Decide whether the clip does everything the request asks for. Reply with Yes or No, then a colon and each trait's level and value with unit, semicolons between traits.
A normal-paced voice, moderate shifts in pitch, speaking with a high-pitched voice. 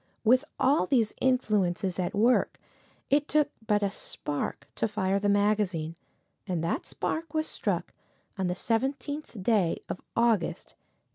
No: average, 145 wpm; wide, 5.7 semitones; high, 210 Hz